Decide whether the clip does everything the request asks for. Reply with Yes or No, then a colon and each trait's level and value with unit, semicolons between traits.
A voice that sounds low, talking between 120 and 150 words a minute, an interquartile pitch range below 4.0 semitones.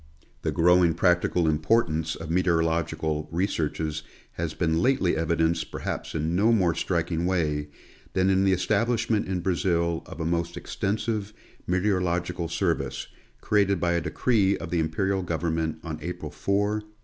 Yes: very low, 85 Hz; average, 145 wpm; average, 2.9 semitones